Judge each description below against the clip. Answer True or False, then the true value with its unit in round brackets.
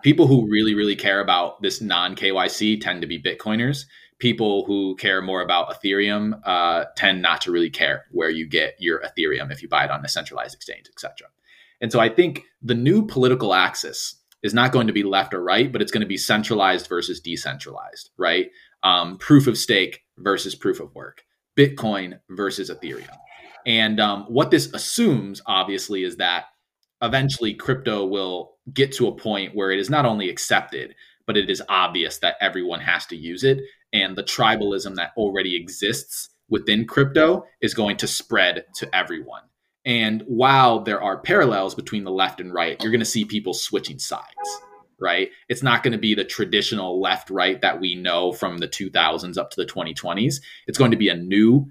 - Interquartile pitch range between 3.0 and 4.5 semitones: False (5.1 semitones)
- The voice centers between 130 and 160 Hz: False (110 Hz)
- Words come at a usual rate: True (190 wpm)